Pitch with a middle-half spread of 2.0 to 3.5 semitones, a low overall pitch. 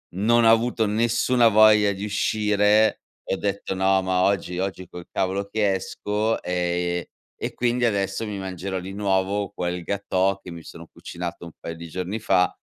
Yes: narrow, 2.5 semitones; low, 100 Hz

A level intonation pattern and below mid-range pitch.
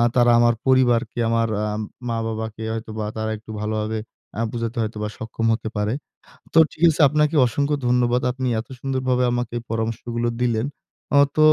Yes: narrow, 1.9 semitones; low, 115 Hz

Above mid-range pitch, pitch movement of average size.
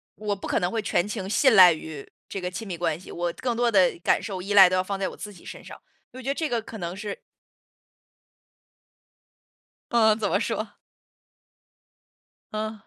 Yes: high, 200 Hz; average, 3.4 semitones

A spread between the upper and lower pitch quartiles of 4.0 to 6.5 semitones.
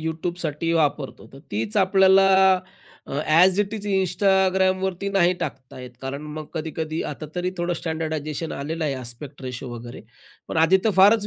Yes: average, 4.3 semitones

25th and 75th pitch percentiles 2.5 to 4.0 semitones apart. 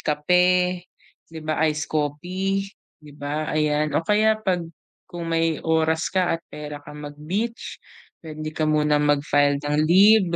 Yes: average, 3.3 semitones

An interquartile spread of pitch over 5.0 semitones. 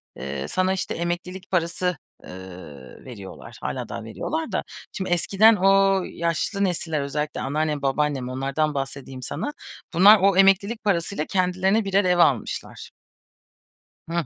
Yes: wide, 5.5 semitones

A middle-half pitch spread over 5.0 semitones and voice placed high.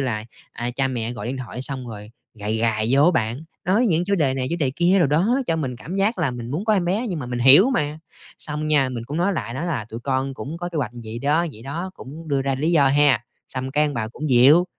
No: wide, 5.4 semitones; medium, 140 Hz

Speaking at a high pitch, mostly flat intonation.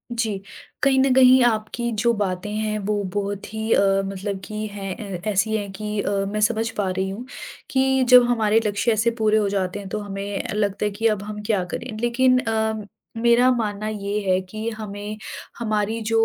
Yes: high, 215 Hz; narrow, 2.1 semitones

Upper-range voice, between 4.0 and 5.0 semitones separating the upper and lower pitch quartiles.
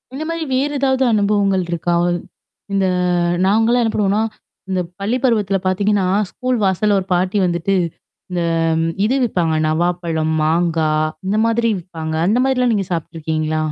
Yes: high, 195 Hz; average, 4.7 semitones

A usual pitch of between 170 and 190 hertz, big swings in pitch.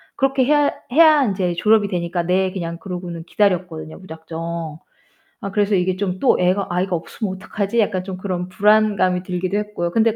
No: medium, 185 Hz; average, 3.0 semitones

